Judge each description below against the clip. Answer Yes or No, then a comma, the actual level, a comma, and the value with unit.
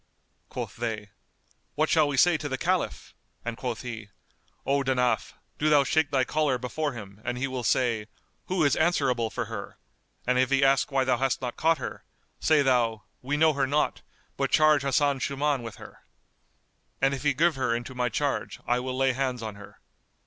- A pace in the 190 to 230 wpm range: Yes, average, 195 wpm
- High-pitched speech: No, low, 130 Hz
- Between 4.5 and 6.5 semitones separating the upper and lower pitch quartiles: No, average, 3.0 semitones